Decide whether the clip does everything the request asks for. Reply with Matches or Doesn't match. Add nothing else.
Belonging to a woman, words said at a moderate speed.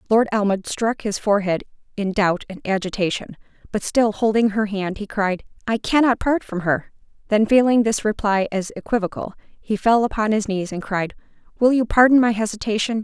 Matches